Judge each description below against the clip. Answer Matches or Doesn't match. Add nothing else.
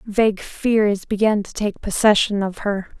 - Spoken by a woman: Matches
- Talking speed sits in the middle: Matches